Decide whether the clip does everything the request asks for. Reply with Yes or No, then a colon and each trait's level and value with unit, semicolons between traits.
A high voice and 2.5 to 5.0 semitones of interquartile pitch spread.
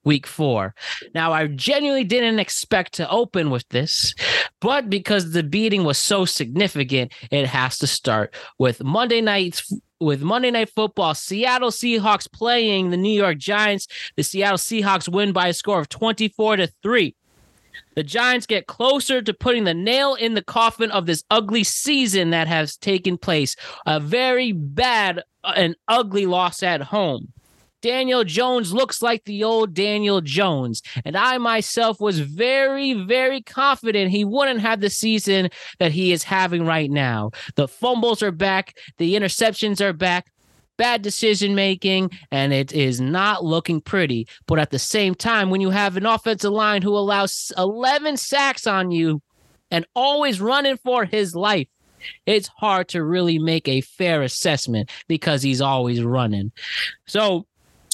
No: high, 195 Hz; wide, 5.6 semitones